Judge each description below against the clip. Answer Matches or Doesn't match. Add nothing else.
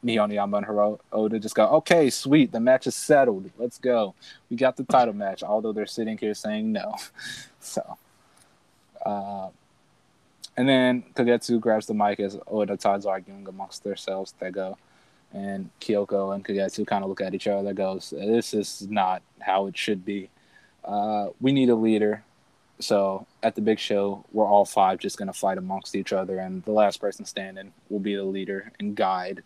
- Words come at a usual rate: Matches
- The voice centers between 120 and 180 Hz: Doesn't match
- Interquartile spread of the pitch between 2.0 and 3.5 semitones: Matches